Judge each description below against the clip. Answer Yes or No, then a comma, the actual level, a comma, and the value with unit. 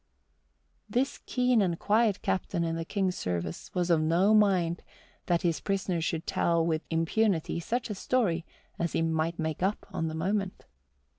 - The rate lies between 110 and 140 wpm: No, average, 165 wpm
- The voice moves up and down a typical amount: Yes, average, 3.7 semitones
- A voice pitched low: No, medium, 175 Hz